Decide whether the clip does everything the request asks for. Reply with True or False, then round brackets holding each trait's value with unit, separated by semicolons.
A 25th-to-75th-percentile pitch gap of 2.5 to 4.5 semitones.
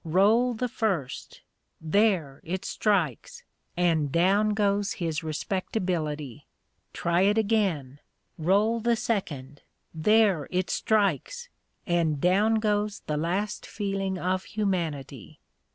False (4.9 semitones)